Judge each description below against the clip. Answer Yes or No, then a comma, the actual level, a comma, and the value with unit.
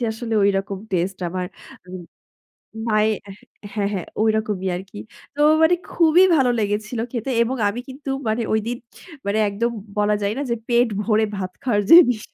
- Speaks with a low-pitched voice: No, high, 215 Hz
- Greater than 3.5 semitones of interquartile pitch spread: No, average, 3.1 semitones